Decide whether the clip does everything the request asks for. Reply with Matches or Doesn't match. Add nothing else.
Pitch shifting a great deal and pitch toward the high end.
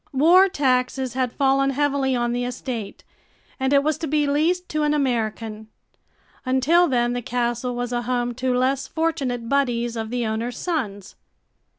Doesn't match